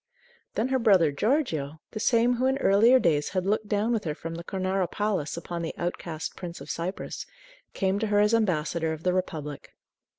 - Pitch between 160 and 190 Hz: Yes, medium, 185 Hz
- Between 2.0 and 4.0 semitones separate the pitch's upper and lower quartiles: No, average, 4.7 semitones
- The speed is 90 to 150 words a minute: No, average, 195 wpm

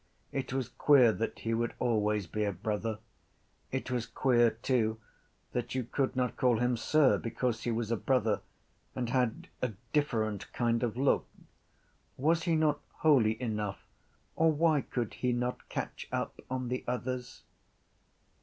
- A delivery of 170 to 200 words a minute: No, average, 155 wpm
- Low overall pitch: Yes, low, 120 Hz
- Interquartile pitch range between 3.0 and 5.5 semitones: No, narrow, 2.6 semitones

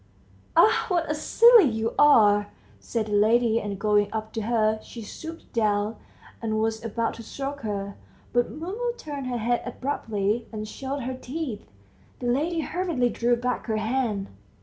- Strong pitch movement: No, average, 4.6 semitones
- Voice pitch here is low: No, high, 235 Hz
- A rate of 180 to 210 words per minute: No, average, 165 wpm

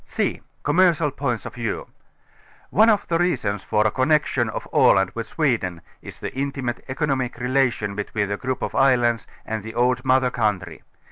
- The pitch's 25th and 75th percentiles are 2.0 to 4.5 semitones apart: Yes, average, 3.9 semitones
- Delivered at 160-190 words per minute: Yes, average, 175 wpm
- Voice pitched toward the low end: Yes, low, 125 Hz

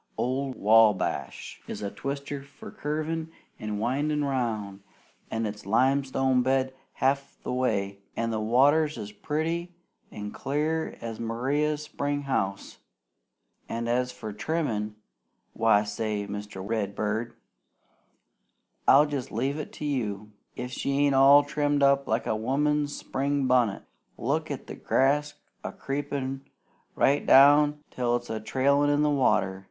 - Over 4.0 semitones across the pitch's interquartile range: Yes, average, 4.8 semitones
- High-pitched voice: No, low, 130 Hz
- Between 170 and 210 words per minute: No, slow, 135 wpm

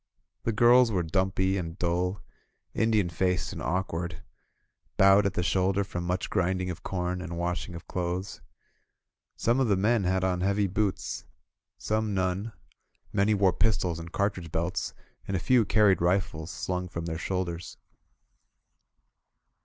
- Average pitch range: No, narrow, 2.1 semitones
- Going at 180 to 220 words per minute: No, average, 155 wpm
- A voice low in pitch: Yes, very low, 95 Hz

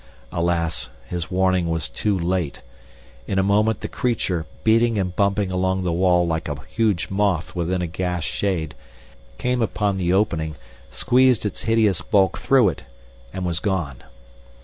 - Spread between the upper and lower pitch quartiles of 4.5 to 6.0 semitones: No, average, 3.3 semitones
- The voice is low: Yes, very low, 95 Hz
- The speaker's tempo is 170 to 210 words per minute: No, average, 155 wpm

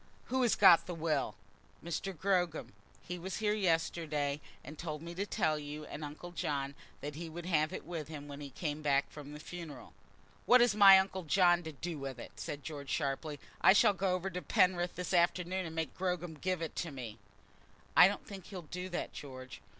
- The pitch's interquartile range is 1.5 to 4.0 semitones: Yes, average, 3.6 semitones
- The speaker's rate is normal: No, fast, 210 wpm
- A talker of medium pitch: Yes, medium, 165 Hz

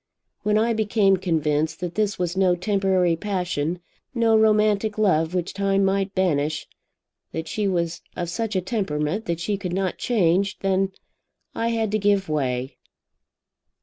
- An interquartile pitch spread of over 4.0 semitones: No, average, 3.5 semitones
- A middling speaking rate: Yes, average, 150 wpm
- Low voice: No, high, 190 Hz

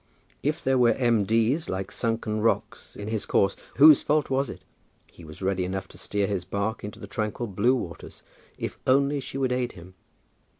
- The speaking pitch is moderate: No, low, 115 Hz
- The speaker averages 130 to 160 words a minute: No, average, 195 wpm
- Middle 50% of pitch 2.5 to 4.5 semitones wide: No, average, 5.0 semitones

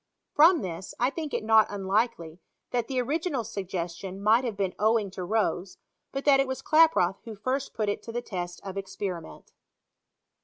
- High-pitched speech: Yes, high, 215 Hz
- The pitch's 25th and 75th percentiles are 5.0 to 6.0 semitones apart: Yes, average, 5.3 semitones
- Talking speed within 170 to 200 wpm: Yes, average, 180 wpm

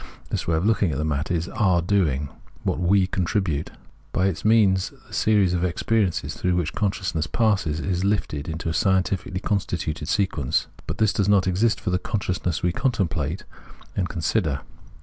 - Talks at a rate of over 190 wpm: No, average, 180 wpm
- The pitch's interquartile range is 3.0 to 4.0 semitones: Yes, average, 3.7 semitones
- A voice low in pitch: Yes, very low, 90 Hz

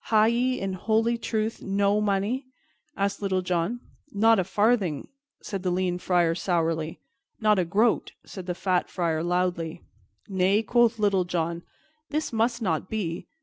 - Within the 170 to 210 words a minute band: No, average, 150 wpm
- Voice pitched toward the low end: No, high, 195 Hz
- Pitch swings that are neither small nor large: Yes, average, 3.7 semitones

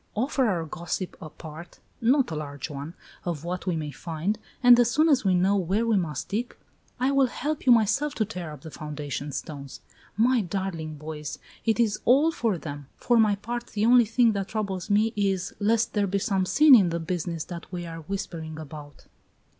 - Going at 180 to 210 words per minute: Yes, average, 200 wpm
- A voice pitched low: No, high, 190 Hz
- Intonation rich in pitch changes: Yes, wide, 6.1 semitones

